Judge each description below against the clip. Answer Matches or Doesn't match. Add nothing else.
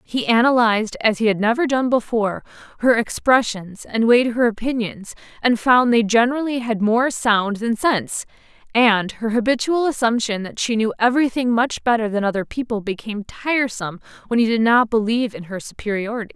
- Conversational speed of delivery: Matches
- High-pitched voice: Matches